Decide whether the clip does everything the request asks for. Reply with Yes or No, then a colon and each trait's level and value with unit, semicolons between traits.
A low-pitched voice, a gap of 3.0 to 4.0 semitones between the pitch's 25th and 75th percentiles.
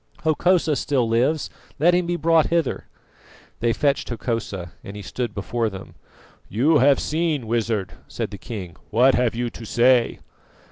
No: low, 125 Hz; average, 5.3 semitones